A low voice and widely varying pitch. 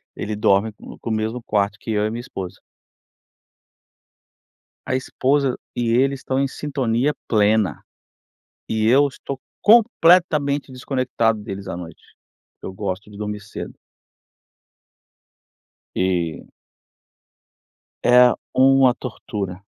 No: low, 115 Hz; average, 4.5 semitones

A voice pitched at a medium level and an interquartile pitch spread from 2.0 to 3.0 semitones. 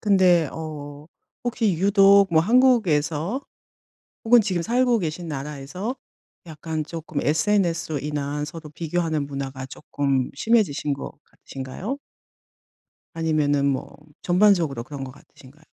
No: medium, 160 Hz; average, 5.3 semitones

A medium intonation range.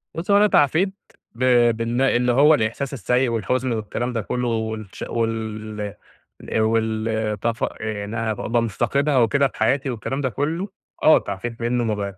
Yes: average, 3.4 semitones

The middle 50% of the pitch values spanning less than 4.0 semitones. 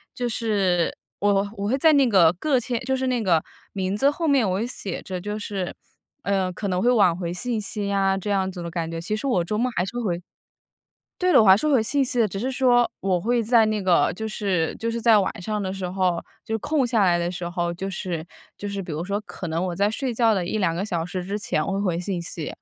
No: average, 4.3 semitones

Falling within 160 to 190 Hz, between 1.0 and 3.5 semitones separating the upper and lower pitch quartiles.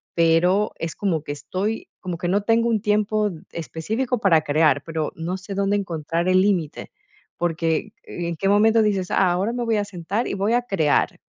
No: medium, 185 Hz; average, 4.1 semitones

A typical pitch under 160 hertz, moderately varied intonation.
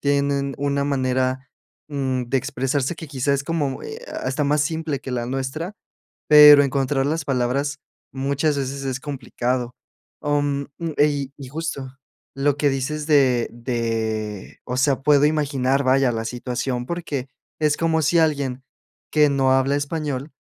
No: medium, 140 Hz; narrow, 2.2 semitones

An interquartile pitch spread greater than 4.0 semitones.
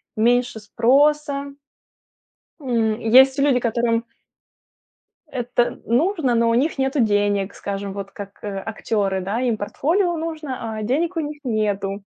Yes: average, 5.1 semitones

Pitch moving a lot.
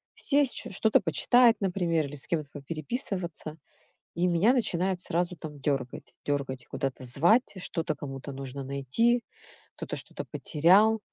Yes: wide, 5.8 semitones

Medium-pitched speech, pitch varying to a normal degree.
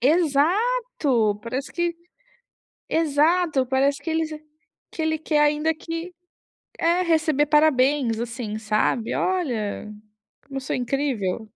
No: very high, 295 Hz; average, 4.6 semitones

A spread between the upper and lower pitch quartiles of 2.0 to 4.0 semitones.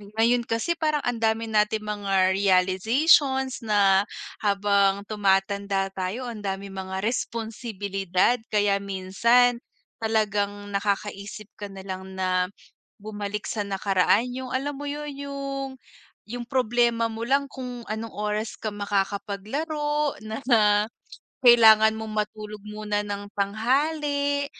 Yes: average, 3.5 semitones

